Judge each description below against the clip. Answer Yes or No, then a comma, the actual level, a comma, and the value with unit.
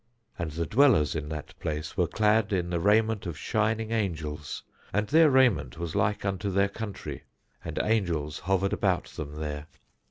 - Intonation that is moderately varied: No, wide, 5.7 semitones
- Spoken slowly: No, average, 165 wpm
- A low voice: Yes, very low, 95 Hz